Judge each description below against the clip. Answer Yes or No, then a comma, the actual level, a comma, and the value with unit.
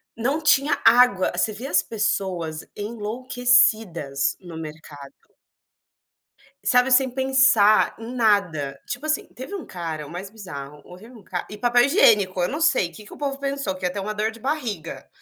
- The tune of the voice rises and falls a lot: Yes, wide, 6.1 semitones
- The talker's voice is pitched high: Yes, high, 215 Hz